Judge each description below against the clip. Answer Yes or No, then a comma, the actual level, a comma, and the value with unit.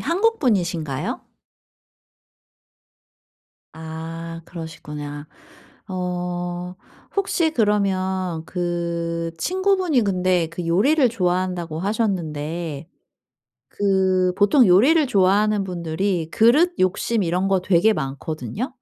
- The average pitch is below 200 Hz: Yes, medium, 185 Hz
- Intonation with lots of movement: No, average, 3.9 semitones